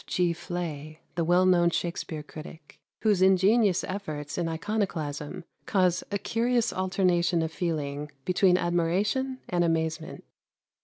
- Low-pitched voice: No, medium, 175 Hz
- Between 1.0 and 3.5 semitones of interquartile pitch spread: Yes, average, 2.9 semitones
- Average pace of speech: No, slow, 115 wpm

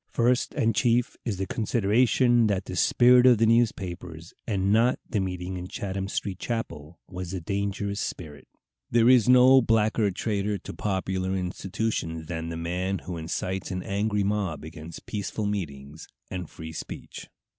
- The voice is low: Yes, low, 100 Hz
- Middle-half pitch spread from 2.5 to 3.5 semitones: No, average, 3.9 semitones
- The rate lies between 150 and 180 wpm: Yes, average, 160 wpm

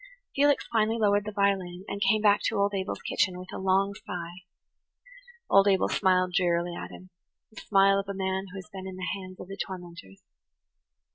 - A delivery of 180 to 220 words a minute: Yes, average, 190 wpm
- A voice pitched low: No, high, 190 Hz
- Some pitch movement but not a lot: No, narrow, 1.6 semitones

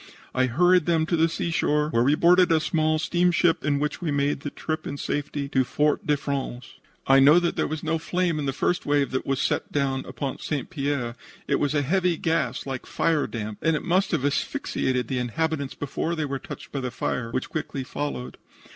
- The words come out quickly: Yes, fast, 210 wpm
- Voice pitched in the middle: Yes, medium, 145 Hz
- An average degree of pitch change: Yes, average, 3.3 semitones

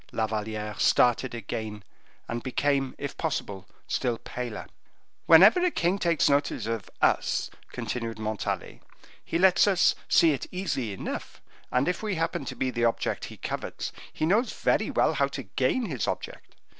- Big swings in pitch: Yes, wide, 7.2 semitones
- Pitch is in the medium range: No, low, 130 Hz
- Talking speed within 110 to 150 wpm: No, average, 160 wpm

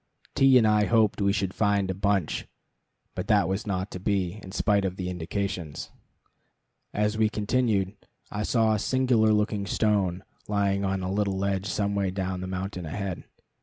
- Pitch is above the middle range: No, low, 100 Hz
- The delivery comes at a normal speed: Yes, average, 175 wpm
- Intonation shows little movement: Yes, narrow, 2.0 semitones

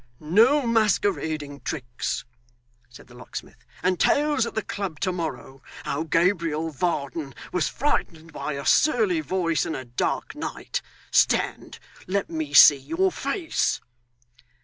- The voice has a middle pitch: Yes, medium, 165 Hz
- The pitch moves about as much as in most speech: No, wide, 7.0 semitones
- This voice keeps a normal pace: No, slow, 130 wpm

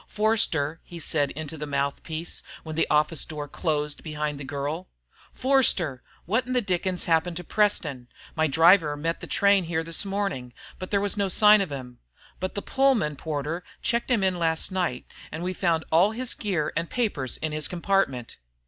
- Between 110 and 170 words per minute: No, average, 185 wpm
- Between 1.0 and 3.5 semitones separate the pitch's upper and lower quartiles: No, average, 4.7 semitones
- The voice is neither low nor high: Yes, medium, 165 Hz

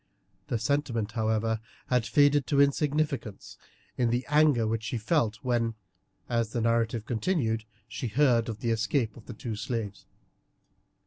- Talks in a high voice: No, low, 115 Hz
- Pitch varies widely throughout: No, average, 3.6 semitones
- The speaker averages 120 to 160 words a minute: Yes, average, 145 wpm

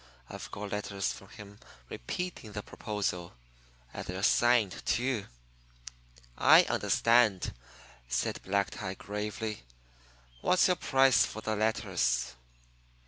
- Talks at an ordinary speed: No, slow, 110 wpm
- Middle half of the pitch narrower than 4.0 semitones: Yes, average, 2.8 semitones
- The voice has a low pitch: Yes, low, 105 Hz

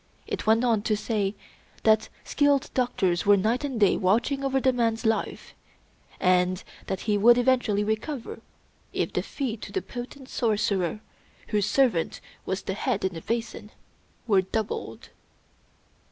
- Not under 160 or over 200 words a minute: No, average, 150 wpm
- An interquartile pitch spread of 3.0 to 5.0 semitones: Yes, average, 3.8 semitones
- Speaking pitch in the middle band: No, high, 220 Hz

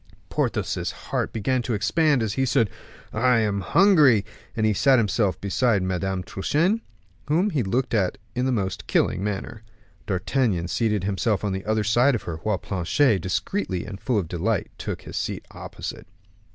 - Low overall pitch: Yes, low, 110 Hz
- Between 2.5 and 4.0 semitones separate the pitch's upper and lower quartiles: No, average, 5.0 semitones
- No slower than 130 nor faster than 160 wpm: No, average, 170 wpm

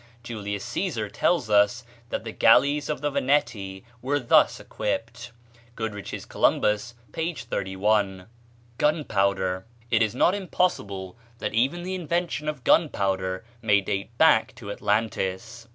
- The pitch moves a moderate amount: No, wide, 6.4 semitones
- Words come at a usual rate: No, slow, 125 wpm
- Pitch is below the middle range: Yes, low, 115 Hz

